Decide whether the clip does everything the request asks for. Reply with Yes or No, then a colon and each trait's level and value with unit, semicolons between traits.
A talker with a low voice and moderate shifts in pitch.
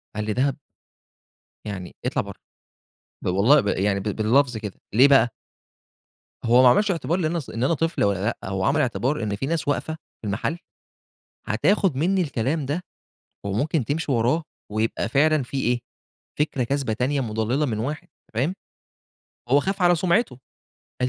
No: low, 130 Hz; wide, 5.8 semitones